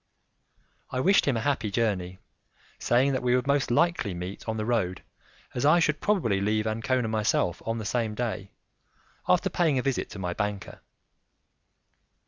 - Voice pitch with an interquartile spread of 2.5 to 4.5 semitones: Yes, average, 4.1 semitones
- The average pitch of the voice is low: Yes, low, 115 Hz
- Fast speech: No, average, 165 wpm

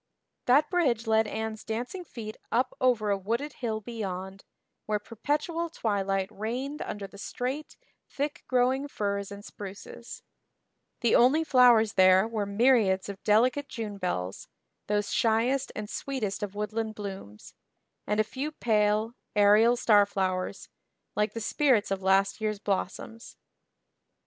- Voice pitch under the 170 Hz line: No, high, 220 Hz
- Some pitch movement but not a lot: Yes, average, 3.5 semitones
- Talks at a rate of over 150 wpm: No, slow, 135 wpm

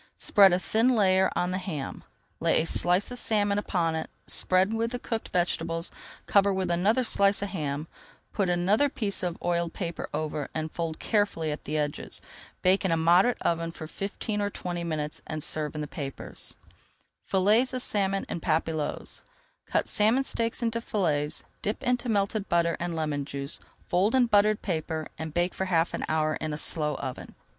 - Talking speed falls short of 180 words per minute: No, average, 185 wpm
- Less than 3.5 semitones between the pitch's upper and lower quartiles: No, average, 4.4 semitones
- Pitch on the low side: No, medium, 180 Hz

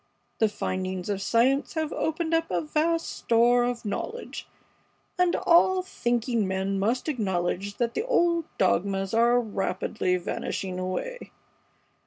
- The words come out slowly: Yes, slow, 130 wpm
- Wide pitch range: Yes, wide, 8.7 semitones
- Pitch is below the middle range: No, high, 235 Hz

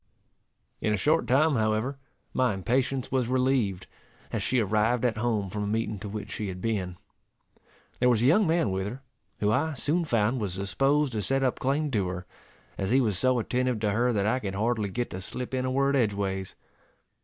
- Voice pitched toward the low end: Yes, low, 115 Hz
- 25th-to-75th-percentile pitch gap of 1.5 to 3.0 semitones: No, average, 4.2 semitones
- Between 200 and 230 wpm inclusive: Yes, fast, 205 wpm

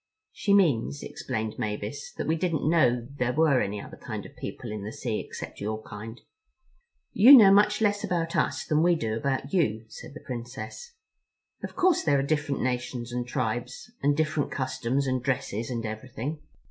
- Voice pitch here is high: No, low, 130 Hz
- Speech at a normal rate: Yes, average, 180 wpm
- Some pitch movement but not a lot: No, wide, 5.9 semitones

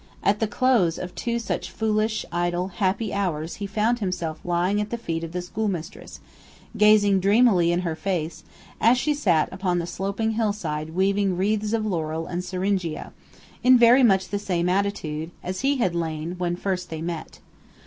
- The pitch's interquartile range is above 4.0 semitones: No, average, 3.6 semitones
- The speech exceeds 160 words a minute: Yes, average, 175 wpm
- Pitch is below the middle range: No, high, 190 Hz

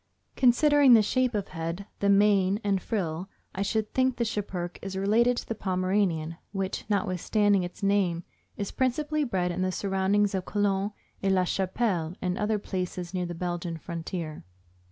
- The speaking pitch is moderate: No, high, 195 Hz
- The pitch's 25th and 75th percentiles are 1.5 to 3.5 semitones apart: Yes, average, 2.7 semitones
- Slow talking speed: No, average, 165 wpm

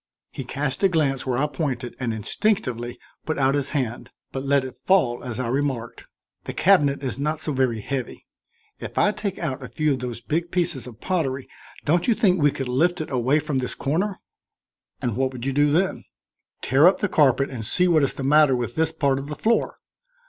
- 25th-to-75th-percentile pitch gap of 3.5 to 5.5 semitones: Yes, average, 3.8 semitones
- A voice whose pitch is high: No, medium, 140 Hz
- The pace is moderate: No, fast, 215 wpm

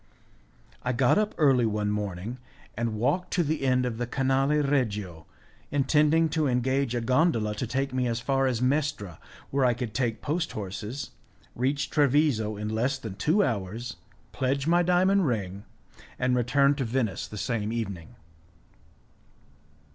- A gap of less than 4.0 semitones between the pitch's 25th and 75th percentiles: No, average, 4.3 semitones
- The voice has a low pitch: Yes, low, 125 Hz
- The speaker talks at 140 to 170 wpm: Yes, average, 155 wpm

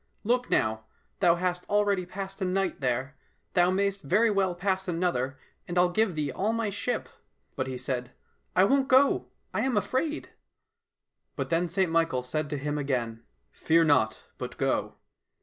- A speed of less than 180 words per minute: No, average, 185 wpm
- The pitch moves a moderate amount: No, wide, 5.9 semitones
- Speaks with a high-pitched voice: No, medium, 180 Hz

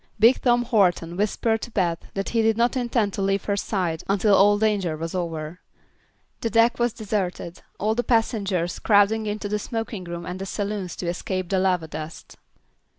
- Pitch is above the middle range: Yes, high, 200 Hz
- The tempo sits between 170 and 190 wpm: Yes, average, 180 wpm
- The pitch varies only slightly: No, average, 3.7 semitones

